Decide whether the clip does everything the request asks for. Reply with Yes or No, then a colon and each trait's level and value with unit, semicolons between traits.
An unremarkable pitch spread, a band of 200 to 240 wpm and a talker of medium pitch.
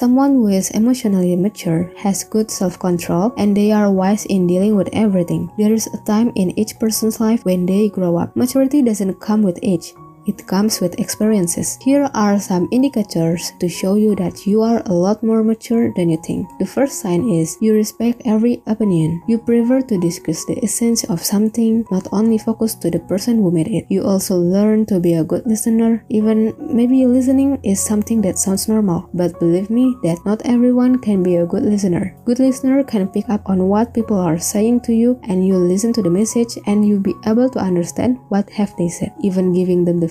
No: average, 3.8 semitones; fast, 205 wpm; high, 210 Hz